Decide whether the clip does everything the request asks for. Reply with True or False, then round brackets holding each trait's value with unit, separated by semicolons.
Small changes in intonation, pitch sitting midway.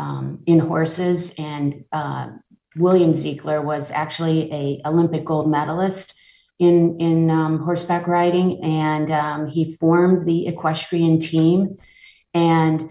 True (2.1 semitones; 160 Hz)